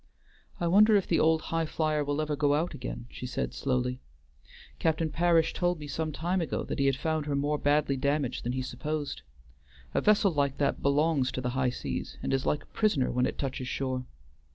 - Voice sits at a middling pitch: Yes, medium, 145 Hz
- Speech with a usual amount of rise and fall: Yes, average, 3.3 semitones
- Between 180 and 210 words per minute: Yes, fast, 205 wpm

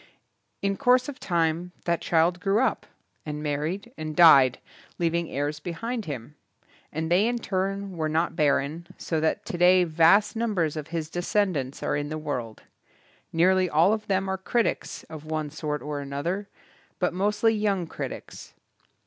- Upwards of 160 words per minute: No, average, 155 wpm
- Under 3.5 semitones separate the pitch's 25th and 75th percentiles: No, average, 4.2 semitones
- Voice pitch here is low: No, medium, 170 Hz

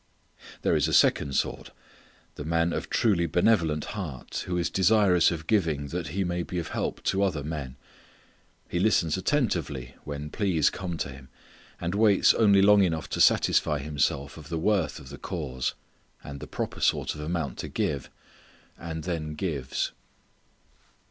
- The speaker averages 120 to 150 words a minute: No, average, 165 wpm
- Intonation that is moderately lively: Yes, average, 4.1 semitones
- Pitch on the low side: Yes, very low, 80 Hz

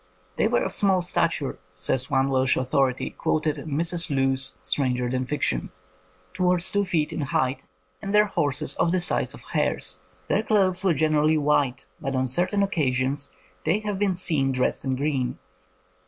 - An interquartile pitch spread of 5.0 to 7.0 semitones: Yes, wide, 5.5 semitones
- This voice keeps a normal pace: Yes, average, 170 wpm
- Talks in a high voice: No, medium, 145 Hz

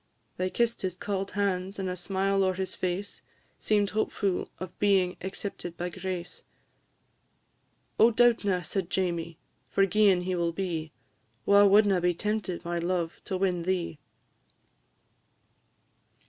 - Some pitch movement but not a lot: No, narrow, 2.1 semitones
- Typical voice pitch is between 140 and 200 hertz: Yes, medium, 185 Hz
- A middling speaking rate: No, slow, 130 wpm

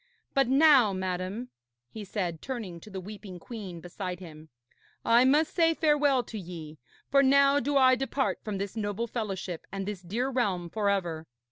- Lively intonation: Yes, wide, 6.2 semitones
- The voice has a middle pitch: No, high, 210 Hz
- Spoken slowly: No, average, 170 wpm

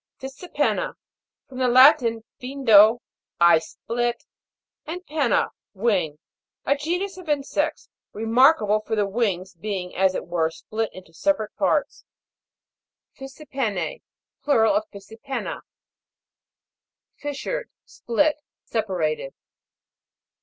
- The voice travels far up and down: Yes, wide, 6.3 semitones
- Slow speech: Yes, slow, 95 wpm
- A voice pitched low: No, high, 235 Hz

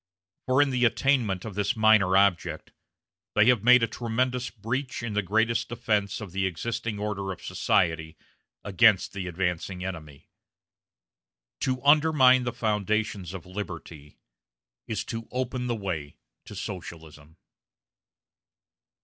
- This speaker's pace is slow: Yes, slow, 130 wpm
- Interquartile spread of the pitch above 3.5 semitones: Yes, average, 4.6 semitones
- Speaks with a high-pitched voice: No, low, 105 Hz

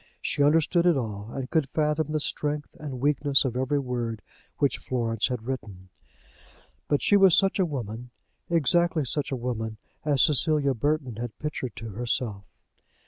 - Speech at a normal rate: Yes, average, 160 wpm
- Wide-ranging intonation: No, average, 4.3 semitones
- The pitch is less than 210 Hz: Yes, low, 135 Hz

